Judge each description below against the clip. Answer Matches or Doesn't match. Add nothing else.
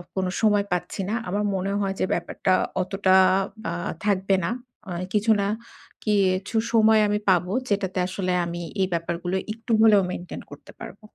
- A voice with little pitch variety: Matches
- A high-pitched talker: Matches